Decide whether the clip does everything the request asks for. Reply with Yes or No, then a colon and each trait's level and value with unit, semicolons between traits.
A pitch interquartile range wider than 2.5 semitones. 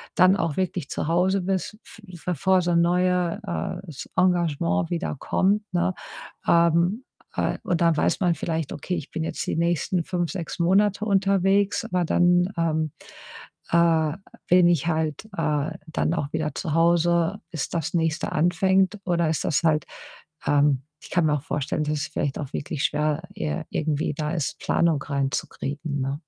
Yes: average, 2.9 semitones